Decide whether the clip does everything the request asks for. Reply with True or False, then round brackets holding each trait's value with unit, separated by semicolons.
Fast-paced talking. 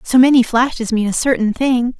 True (210 wpm)